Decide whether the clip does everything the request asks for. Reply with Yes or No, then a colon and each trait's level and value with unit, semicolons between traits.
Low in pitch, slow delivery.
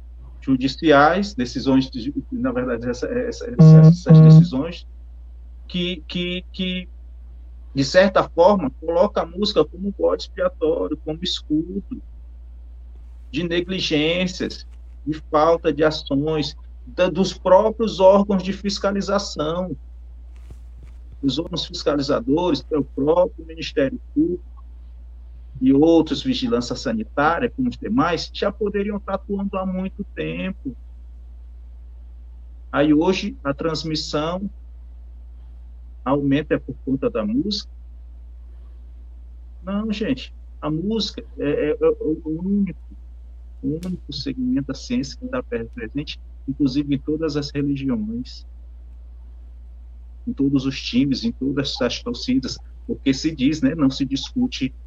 No: medium, 150 Hz; slow, 115 wpm